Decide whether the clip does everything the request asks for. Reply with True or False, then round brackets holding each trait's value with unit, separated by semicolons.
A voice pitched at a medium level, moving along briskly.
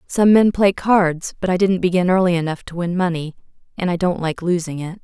True (180 Hz; 225 wpm)